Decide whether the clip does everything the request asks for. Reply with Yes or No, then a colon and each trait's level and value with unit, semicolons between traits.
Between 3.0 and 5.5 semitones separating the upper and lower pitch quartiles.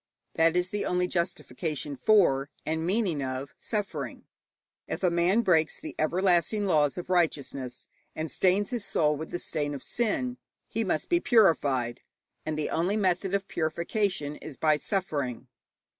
Yes: average, 4.6 semitones